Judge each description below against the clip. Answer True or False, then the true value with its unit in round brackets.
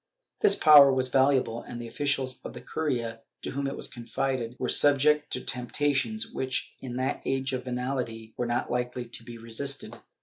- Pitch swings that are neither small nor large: False (2.3 semitones)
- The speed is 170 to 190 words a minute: True (180 wpm)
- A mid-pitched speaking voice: False (130 Hz)